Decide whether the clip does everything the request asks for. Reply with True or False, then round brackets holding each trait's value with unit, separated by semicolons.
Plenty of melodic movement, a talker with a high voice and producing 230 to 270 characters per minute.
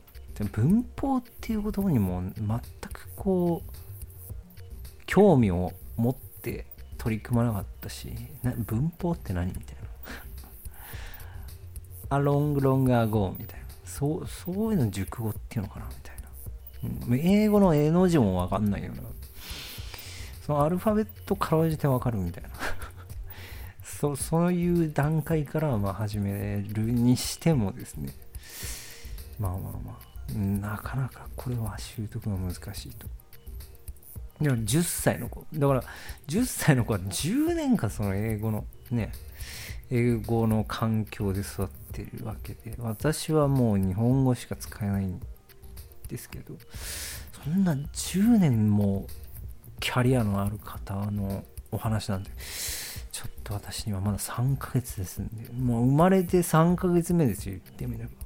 False (6.3 semitones; 105 Hz; 260 characters per minute)